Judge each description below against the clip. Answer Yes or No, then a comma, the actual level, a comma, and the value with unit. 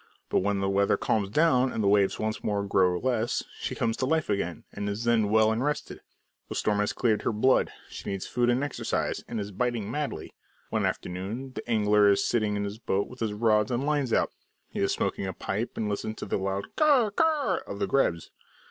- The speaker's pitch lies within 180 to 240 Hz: No, low, 110 Hz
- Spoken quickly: Yes, fast, 225 wpm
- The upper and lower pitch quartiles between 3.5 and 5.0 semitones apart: Yes, average, 3.8 semitones